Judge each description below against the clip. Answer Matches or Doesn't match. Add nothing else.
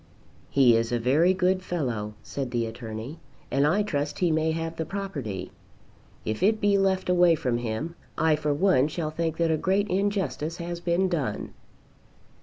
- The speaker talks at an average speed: Matches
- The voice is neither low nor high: Matches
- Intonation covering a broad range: Matches